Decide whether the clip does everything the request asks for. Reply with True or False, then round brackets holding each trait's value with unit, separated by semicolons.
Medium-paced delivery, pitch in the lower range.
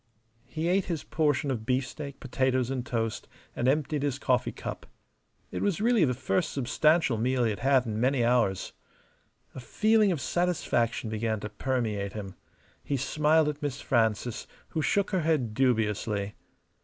True (160 wpm; 130 Hz)